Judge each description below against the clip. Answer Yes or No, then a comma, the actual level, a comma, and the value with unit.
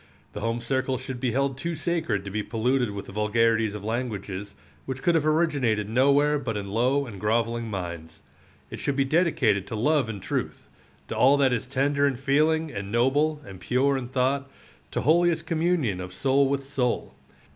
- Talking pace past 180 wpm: Yes, average, 190 wpm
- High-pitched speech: No, low, 130 Hz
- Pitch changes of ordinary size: Yes, average, 4.6 semitones